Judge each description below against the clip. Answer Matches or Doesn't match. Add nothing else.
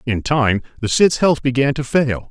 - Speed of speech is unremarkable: Doesn't match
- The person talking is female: Doesn't match